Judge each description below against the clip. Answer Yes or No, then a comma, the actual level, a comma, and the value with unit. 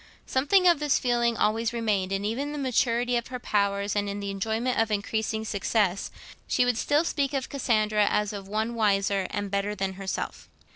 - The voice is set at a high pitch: Yes, high, 220 Hz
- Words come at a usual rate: Yes, average, 195 wpm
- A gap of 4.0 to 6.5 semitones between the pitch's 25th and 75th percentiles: No, average, 3.5 semitones